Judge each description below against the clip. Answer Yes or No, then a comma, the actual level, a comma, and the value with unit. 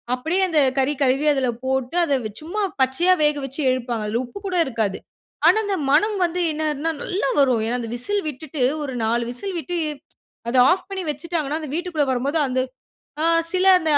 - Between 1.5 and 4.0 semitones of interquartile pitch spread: No, average, 5.2 semitones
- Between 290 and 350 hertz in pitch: Yes, very high, 295 Hz